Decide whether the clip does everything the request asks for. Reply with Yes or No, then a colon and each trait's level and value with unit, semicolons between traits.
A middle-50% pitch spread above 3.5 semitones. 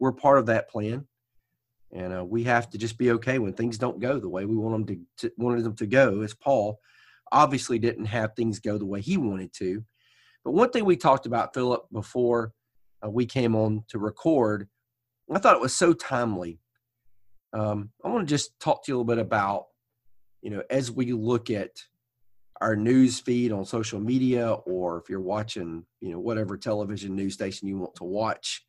No: average, 2.7 semitones